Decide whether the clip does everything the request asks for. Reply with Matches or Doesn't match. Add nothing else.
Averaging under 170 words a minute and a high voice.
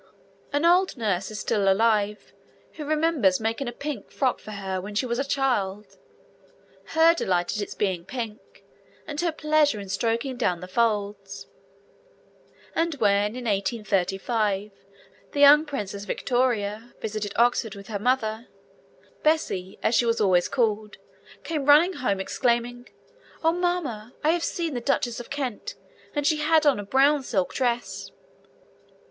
Matches